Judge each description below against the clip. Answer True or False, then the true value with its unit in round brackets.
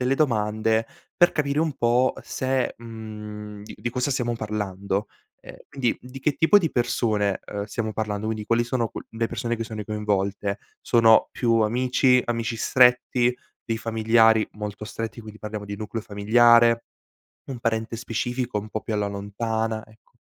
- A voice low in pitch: True (115 Hz)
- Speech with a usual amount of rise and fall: False (2.2 semitones)